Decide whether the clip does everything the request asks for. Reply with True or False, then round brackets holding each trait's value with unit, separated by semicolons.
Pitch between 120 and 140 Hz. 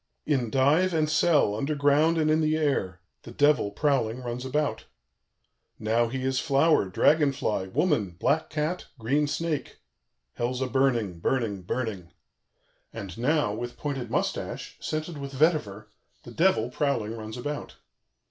True (135 Hz)